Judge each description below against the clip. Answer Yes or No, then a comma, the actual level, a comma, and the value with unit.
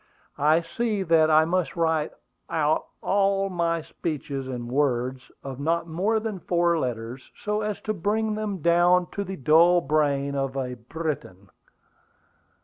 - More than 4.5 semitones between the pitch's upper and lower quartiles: Yes, average, 5.1 semitones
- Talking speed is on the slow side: No, average, 150 wpm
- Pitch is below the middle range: No, medium, 165 Hz